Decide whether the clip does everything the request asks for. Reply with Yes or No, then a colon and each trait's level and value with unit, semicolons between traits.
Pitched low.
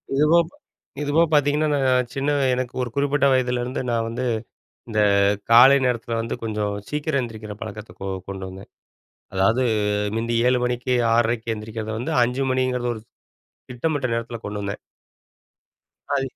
Yes: low, 120 Hz